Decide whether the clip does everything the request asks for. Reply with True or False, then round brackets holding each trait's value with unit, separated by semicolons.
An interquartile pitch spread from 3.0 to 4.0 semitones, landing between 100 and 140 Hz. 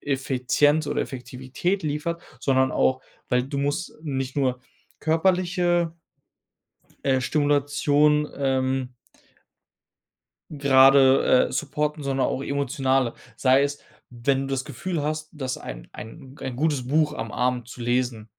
False (2.5 semitones; 135 Hz)